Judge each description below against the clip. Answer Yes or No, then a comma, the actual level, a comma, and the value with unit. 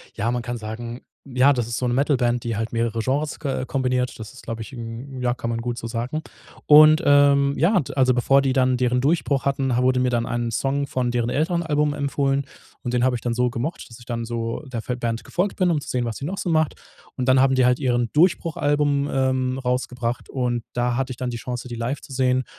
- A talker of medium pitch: No, low, 125 Hz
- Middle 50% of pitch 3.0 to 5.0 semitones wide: No, narrow, 2.6 semitones